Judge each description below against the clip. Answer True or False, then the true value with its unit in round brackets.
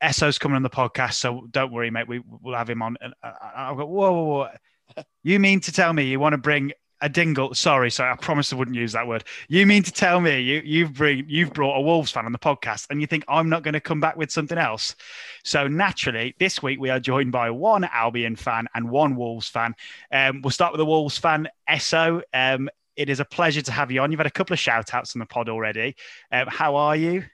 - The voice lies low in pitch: False (145 Hz)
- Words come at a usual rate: False (250 wpm)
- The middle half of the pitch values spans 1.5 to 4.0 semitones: False (4.6 semitones)